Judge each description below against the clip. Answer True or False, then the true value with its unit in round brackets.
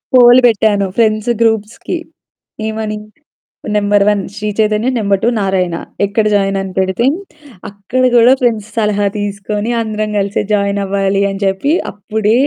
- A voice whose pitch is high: True (210 Hz)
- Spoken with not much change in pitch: True (1.7 semitones)